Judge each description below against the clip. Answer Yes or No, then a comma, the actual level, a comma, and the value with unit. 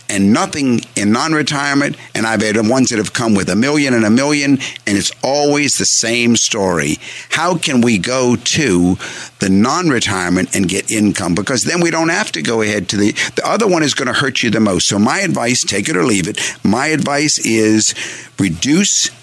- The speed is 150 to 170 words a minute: No, fast, 205 wpm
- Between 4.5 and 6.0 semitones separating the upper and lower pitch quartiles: Yes, average, 5.2 semitones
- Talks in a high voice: No, low, 115 Hz